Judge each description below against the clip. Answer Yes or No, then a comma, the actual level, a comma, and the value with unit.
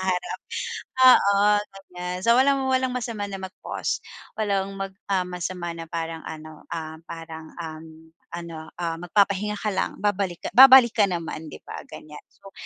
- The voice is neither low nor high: Yes, medium, 180 Hz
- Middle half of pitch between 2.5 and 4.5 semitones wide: Yes, average, 3.8 semitones